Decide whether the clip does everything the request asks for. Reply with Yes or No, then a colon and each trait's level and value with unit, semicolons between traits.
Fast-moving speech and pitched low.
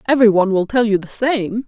No: fast, 250 wpm; high, 220 Hz